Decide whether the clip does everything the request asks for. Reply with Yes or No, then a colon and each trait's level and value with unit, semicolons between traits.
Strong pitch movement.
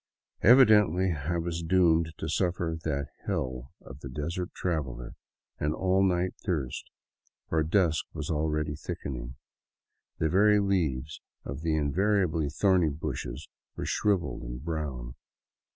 No: average, 4.1 semitones